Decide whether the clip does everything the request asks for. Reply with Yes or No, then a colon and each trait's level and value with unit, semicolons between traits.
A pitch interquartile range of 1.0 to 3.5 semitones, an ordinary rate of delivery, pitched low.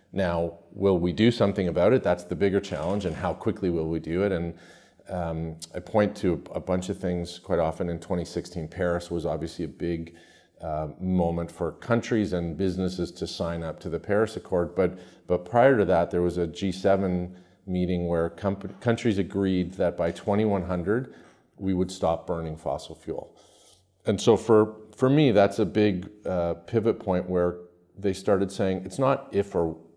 Yes: narrow, 2.4 semitones; average, 180 wpm; very low, 90 Hz